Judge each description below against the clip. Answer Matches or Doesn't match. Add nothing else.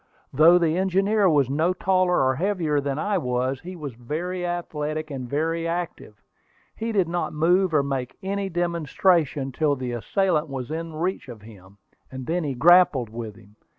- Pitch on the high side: Doesn't match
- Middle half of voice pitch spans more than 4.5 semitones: Matches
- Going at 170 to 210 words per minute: Matches